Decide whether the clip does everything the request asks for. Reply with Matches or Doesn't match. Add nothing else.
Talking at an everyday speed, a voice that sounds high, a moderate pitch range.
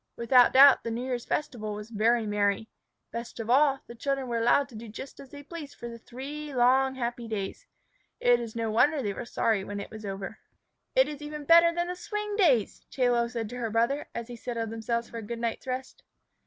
Doesn't match